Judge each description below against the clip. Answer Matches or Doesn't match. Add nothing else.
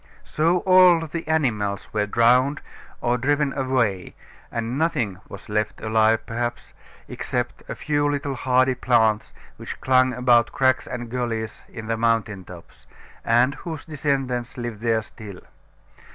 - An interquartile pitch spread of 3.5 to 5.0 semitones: Matches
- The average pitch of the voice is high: Doesn't match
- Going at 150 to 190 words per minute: Doesn't match